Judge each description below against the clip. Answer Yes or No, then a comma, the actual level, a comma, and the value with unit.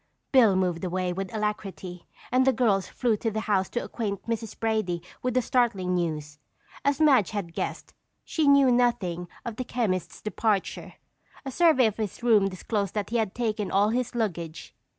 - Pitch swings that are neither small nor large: Yes, average, 4.5 semitones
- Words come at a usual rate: Yes, average, 175 wpm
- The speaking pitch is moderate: No, high, 215 Hz